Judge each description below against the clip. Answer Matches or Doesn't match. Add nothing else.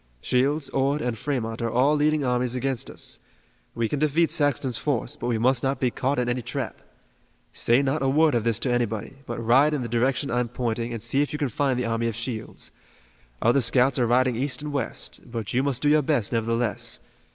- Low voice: Matches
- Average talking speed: Doesn't match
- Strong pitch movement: Doesn't match